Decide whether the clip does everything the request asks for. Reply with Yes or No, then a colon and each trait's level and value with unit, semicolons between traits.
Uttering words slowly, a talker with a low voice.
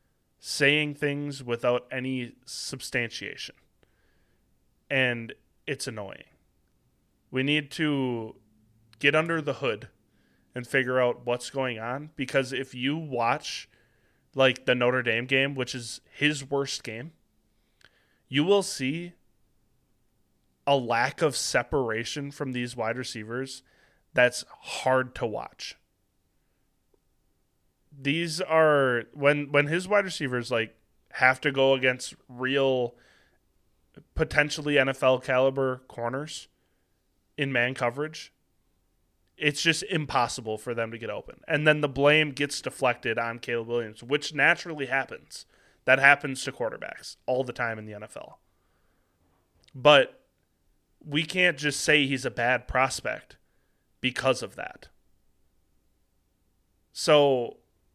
Yes: slow, 115 wpm; low, 130 Hz